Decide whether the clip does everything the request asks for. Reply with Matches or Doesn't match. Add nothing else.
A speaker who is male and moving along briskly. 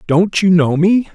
Matches